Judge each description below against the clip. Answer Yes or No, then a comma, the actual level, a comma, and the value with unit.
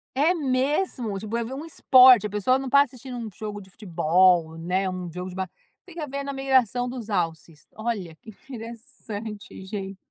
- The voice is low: No, high, 220 Hz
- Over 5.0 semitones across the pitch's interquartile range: Yes, wide, 5.6 semitones